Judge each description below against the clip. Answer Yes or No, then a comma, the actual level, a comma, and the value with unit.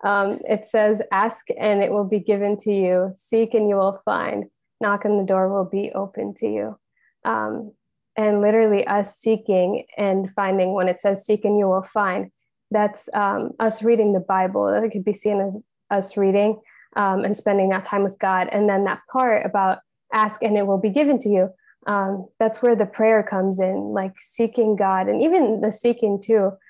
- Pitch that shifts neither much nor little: No, narrow, 1.8 semitones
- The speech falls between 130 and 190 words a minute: No, average, 200 wpm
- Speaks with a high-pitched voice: Yes, high, 205 Hz